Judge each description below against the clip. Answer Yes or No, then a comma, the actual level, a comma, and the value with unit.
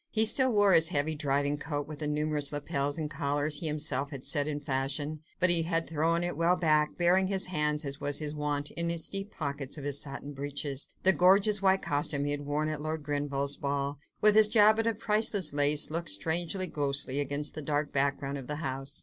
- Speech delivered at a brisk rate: Yes, fast, 215 wpm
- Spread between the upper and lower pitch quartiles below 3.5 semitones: Yes, average, 3.0 semitones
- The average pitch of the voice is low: No, medium, 150 Hz